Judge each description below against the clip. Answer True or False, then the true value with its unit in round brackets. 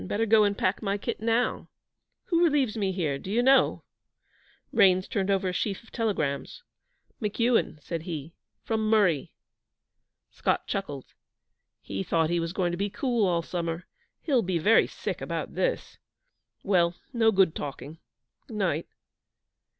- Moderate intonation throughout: True (4.8 semitones)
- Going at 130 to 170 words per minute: True (150 wpm)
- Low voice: False (195 Hz)